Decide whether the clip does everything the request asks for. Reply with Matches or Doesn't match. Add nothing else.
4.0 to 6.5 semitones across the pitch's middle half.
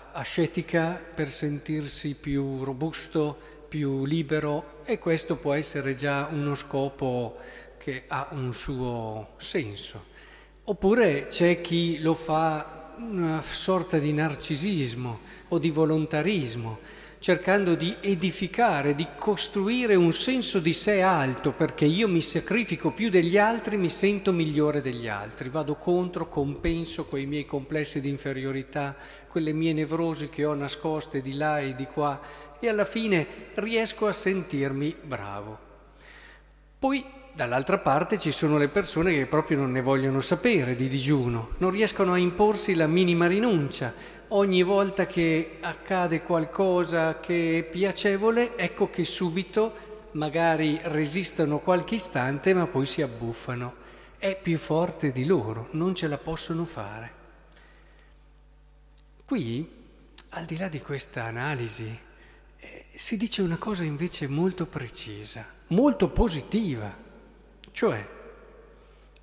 Matches